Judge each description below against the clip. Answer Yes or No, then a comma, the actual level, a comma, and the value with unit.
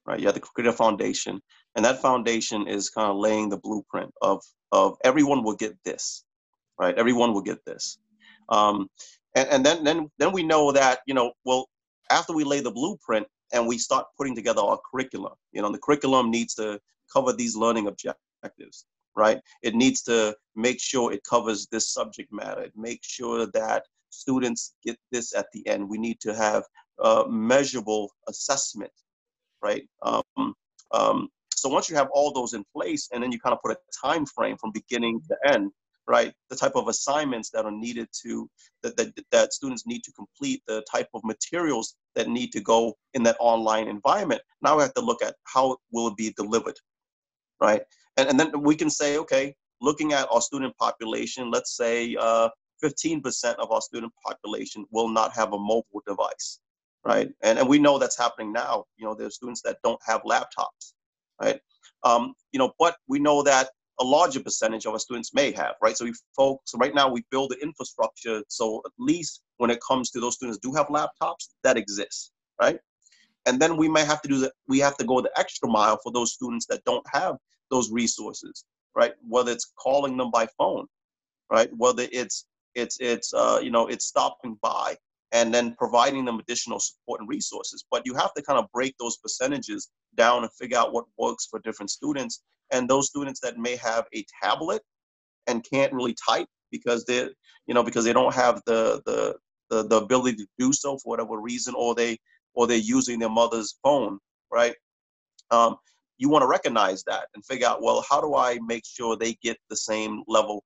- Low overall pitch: Yes, low, 120 Hz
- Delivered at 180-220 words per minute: Yes, average, 200 wpm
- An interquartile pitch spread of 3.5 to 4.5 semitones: Yes, average, 4.0 semitones